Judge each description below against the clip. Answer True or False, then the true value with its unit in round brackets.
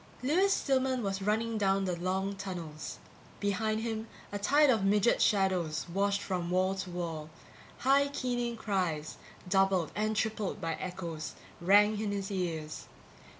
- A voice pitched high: True (195 Hz)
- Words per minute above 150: False (145 wpm)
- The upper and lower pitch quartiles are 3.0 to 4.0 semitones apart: True (3.4 semitones)